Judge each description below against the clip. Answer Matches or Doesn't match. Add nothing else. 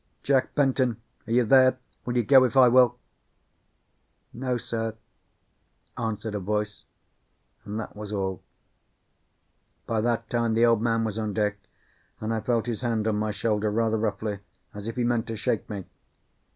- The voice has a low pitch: Matches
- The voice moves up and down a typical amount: Doesn't match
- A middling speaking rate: Matches